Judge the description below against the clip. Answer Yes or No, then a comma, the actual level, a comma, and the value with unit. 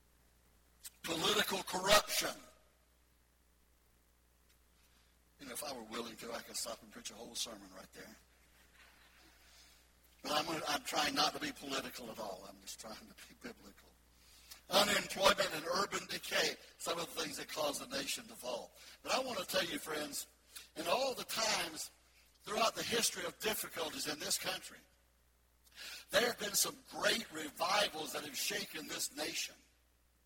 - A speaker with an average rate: Yes, average, 155 wpm